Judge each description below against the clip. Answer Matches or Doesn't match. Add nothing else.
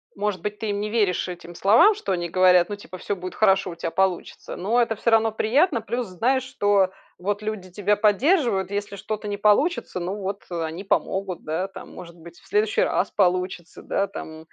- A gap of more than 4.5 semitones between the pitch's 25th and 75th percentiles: Doesn't match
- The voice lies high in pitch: Matches